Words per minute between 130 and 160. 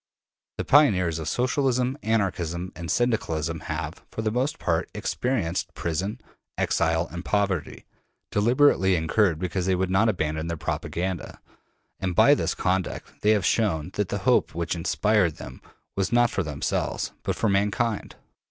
Yes: average, 150 wpm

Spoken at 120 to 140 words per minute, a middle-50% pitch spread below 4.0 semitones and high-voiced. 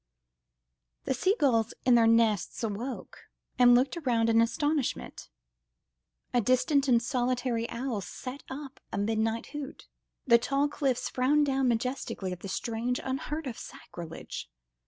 Yes: slow, 135 wpm; average, 3.0 semitones; high, 245 Hz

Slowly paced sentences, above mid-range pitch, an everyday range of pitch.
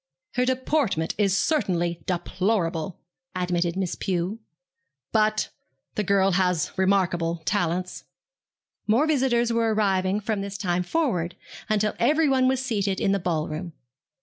Yes: slow, 125 wpm; high, 195 Hz; average, 4.2 semitones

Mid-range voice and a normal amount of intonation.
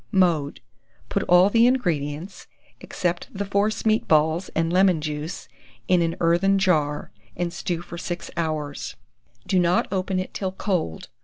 Yes: medium, 175 Hz; average, 3.2 semitones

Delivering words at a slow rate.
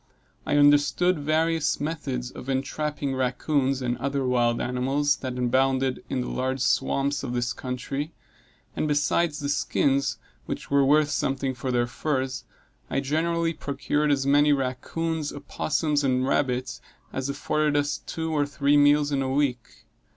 No: average, 150 wpm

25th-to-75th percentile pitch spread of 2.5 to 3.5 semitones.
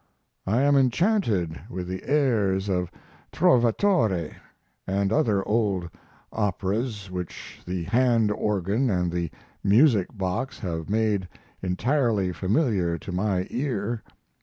No: average, 4.4 semitones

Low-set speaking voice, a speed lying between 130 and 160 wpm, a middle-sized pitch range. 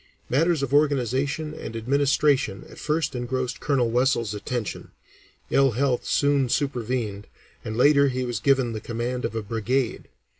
Yes: low, 130 Hz; average, 145 wpm; average, 3.3 semitones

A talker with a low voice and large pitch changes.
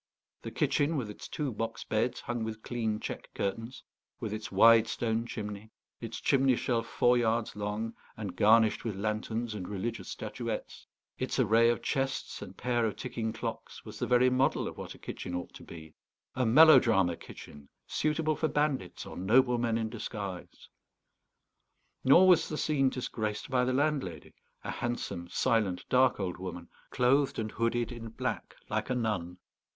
No: low, 115 Hz; average, 3.3 semitones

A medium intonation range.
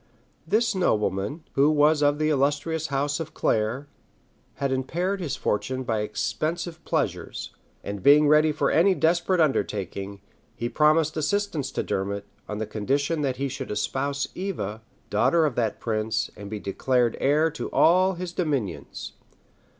No: wide, 6.2 semitones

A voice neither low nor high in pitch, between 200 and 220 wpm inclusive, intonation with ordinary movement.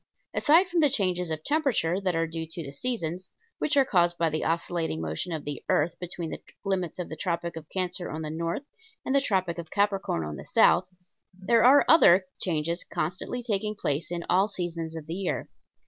Yes: medium, 175 Hz; fast, 205 wpm; average, 3.5 semitones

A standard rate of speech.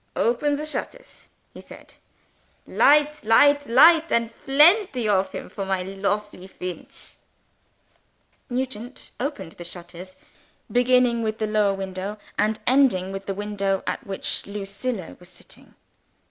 No: slow, 130 wpm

